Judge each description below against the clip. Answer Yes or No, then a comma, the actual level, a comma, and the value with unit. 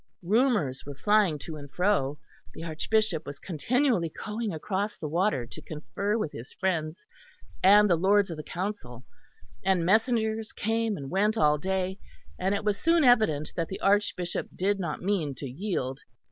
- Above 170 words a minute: No, average, 165 wpm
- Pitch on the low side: No, high, 190 Hz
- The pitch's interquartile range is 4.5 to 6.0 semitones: Yes, average, 5.3 semitones